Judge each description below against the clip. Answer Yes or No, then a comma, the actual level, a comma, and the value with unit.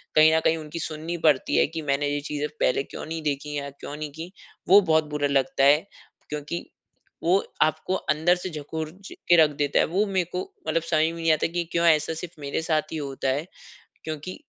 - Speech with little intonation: Yes, narrow, 2.2 semitones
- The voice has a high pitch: No, medium, 155 Hz